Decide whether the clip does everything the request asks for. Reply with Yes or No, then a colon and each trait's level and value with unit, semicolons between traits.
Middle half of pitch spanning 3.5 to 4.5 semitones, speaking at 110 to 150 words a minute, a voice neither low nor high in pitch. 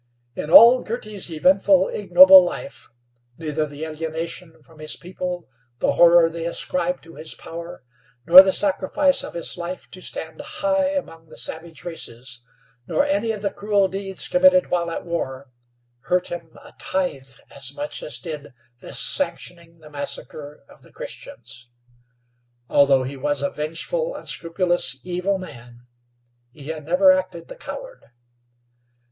Yes: average, 3.9 semitones; average, 145 wpm; medium, 170 Hz